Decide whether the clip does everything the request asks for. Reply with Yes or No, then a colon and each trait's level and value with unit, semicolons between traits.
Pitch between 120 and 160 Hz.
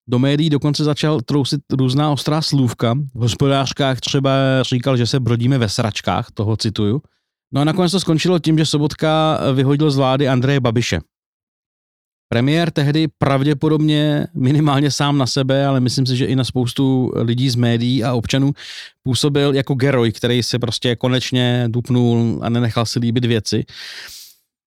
Yes: low, 135 Hz